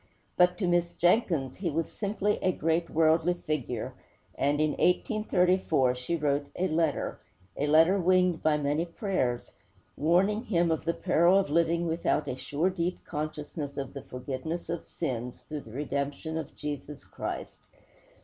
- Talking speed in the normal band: Yes, average, 155 wpm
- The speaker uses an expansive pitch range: No, average, 3.5 semitones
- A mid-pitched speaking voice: Yes, medium, 160 Hz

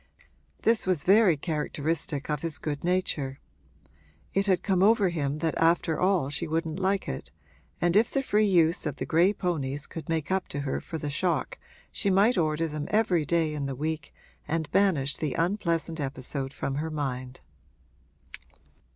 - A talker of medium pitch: Yes, medium, 160 Hz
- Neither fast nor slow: Yes, average, 170 wpm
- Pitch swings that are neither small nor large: Yes, average, 4.1 semitones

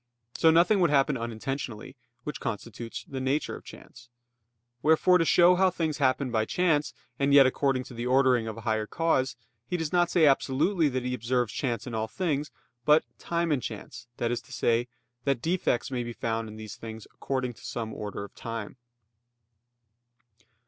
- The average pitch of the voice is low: Yes, low, 130 Hz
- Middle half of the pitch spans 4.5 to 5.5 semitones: Yes, average, 4.8 semitones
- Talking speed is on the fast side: No, average, 185 wpm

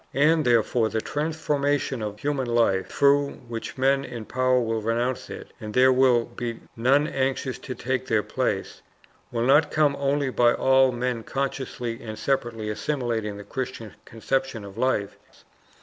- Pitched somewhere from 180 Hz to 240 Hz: No, low, 125 Hz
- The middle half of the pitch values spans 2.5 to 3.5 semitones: Yes, average, 3.0 semitones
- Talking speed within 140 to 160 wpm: Yes, average, 155 wpm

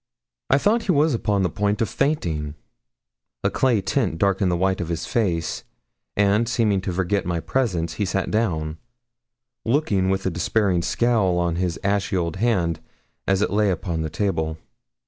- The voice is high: No, very low, 95 Hz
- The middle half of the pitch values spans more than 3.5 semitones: Yes, average, 4.0 semitones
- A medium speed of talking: Yes, average, 170 wpm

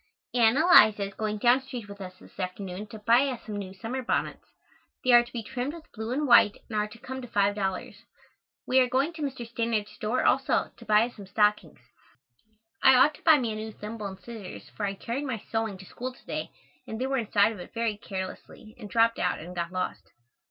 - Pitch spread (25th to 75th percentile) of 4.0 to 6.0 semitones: No, average, 3.5 semitones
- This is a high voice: Yes, high, 220 Hz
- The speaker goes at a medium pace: No, fast, 230 wpm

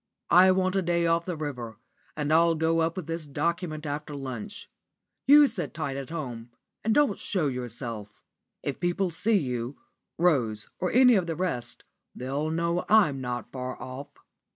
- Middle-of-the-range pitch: Yes, medium, 160 Hz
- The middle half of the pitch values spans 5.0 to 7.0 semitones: Yes, wide, 5.4 semitones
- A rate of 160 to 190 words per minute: Yes, average, 170 wpm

